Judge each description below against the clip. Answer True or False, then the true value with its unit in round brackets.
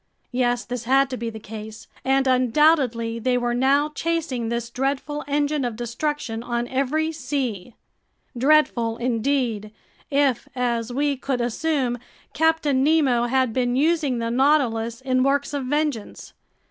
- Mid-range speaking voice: False (255 Hz)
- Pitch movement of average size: True (3.2 semitones)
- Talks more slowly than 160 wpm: True (140 wpm)